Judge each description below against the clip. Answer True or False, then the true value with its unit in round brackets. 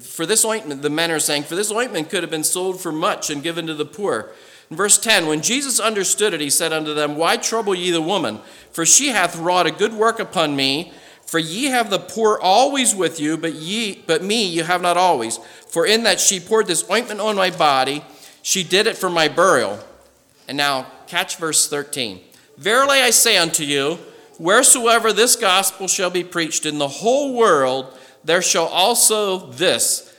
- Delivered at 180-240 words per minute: True (205 wpm)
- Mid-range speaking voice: True (180 Hz)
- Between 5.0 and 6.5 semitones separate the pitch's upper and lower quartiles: True (5.5 semitones)